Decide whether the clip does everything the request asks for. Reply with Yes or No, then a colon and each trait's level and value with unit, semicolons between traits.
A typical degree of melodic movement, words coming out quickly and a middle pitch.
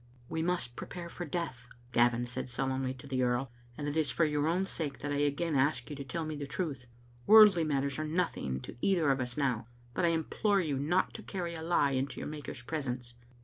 Yes: average, 4.2 semitones; fast, 225 wpm; medium, 145 Hz